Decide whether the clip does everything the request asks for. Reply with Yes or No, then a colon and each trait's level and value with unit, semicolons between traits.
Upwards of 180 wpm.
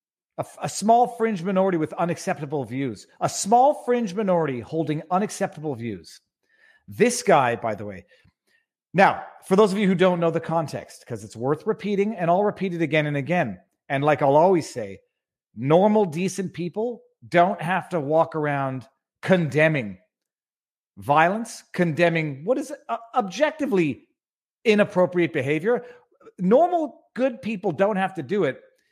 No: average, 145 wpm